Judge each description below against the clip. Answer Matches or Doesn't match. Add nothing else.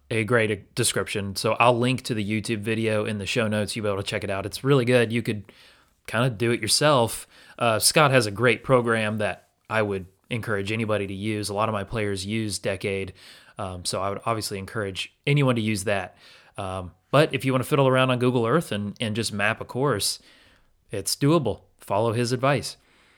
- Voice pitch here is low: Matches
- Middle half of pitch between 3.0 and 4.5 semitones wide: Matches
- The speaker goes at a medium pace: Doesn't match